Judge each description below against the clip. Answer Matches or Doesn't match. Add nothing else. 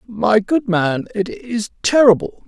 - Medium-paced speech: Matches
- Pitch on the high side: Matches